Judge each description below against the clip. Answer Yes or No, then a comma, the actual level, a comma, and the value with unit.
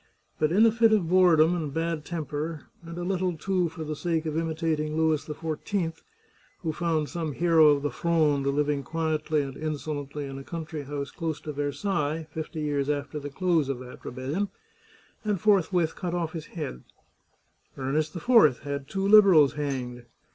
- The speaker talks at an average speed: Yes, average, 170 wpm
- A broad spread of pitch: No, average, 2.8 semitones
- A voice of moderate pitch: Yes, medium, 155 Hz